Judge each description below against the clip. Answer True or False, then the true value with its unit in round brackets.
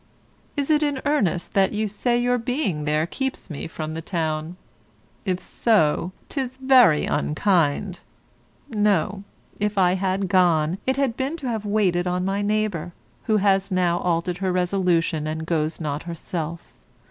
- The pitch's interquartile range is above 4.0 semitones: True (4.4 semitones)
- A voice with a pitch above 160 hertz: True (185 Hz)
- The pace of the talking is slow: False (155 wpm)